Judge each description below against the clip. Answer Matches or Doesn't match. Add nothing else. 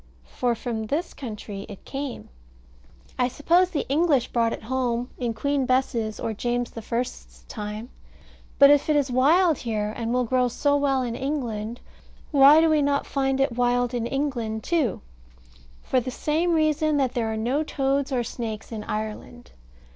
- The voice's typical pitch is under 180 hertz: Doesn't match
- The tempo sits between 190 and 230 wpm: Doesn't match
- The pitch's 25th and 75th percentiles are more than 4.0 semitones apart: Doesn't match